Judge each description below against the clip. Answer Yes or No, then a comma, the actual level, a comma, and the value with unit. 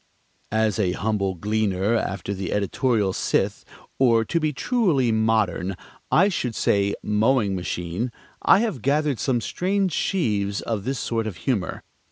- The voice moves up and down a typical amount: Yes, average, 5.0 semitones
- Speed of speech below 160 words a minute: Yes, average, 145 wpm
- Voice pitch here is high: No, low, 110 Hz